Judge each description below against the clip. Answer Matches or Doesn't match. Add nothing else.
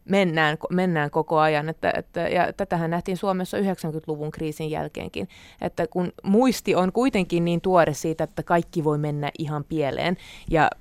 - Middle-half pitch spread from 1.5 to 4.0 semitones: Matches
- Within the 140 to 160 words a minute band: Matches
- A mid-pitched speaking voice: Matches